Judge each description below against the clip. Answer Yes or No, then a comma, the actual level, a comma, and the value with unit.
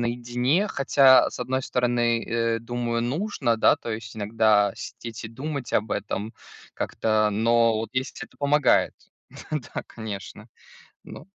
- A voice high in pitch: No, low, 115 Hz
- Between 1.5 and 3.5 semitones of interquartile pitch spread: Yes, narrow, 2.6 semitones